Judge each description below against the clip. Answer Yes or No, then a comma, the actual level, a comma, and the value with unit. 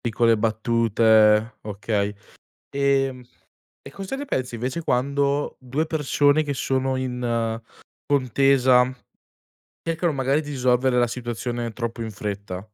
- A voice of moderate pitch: No, low, 125 Hz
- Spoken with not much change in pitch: No, average, 3.3 semitones